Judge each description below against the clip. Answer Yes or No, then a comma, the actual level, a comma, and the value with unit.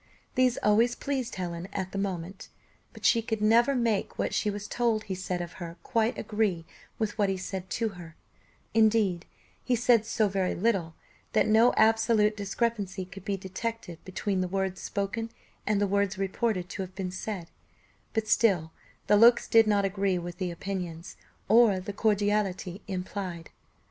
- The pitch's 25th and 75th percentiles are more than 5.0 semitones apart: No, average, 3.1 semitones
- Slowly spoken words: No, average, 170 wpm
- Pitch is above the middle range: Yes, high, 200 Hz